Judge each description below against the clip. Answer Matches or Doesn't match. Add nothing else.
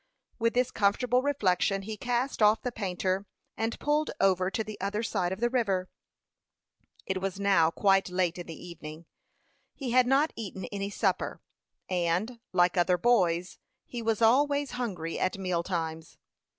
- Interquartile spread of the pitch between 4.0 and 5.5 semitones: Matches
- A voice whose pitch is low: Doesn't match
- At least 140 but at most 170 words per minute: Matches